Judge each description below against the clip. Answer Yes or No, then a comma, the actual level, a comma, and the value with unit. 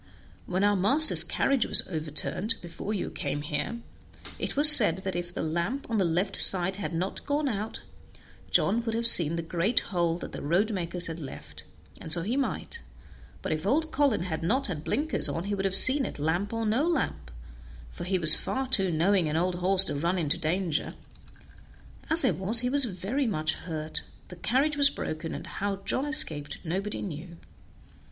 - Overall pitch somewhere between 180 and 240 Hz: Yes, high, 190 Hz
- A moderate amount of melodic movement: No, wide, 5.7 semitones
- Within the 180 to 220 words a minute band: Yes, average, 195 wpm